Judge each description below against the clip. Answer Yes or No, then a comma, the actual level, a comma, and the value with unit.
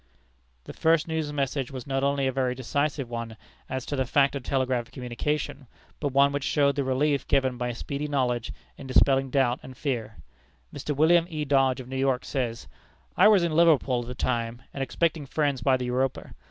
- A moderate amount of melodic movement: No, narrow, 2.3 semitones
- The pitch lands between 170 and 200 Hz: No, low, 135 Hz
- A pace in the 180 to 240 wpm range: Yes, average, 195 wpm